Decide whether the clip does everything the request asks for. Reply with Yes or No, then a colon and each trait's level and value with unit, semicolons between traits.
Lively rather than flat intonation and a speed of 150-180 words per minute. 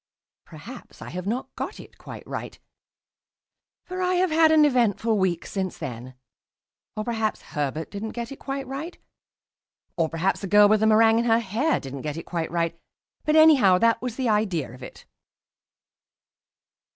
Yes: wide, 6.9 semitones; average, 170 wpm